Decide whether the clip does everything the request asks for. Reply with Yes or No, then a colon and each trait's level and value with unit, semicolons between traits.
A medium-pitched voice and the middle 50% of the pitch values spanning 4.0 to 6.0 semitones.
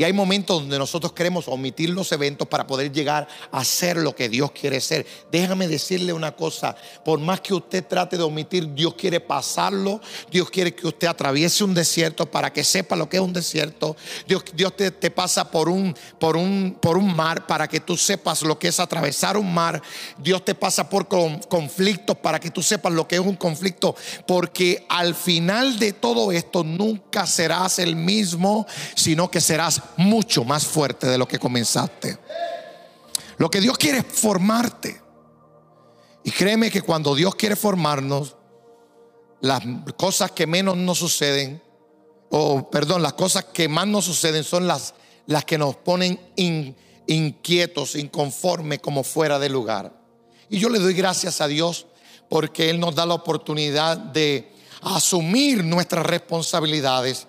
No: medium, 170 Hz; average, 3.5 semitones